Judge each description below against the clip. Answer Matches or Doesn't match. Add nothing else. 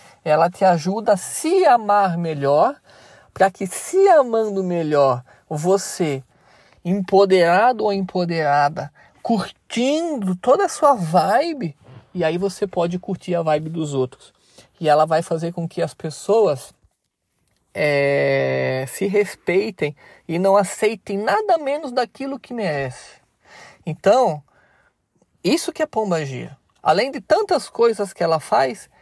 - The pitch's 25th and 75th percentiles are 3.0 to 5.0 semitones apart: Doesn't match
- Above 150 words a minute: Doesn't match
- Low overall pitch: Doesn't match